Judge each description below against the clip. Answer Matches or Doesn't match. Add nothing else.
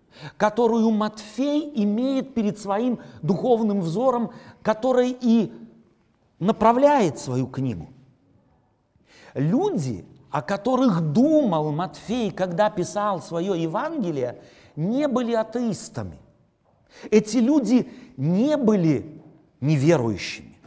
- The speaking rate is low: Matches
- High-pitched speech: Matches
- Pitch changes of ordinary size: Doesn't match